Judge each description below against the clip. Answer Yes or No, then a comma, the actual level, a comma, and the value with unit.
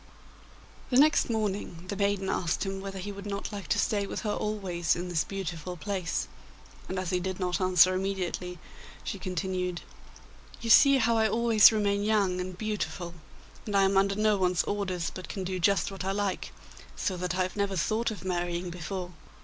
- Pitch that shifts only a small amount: Yes, narrow, 2.1 semitones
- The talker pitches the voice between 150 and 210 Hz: Yes, high, 190 Hz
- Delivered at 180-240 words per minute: Yes, average, 190 wpm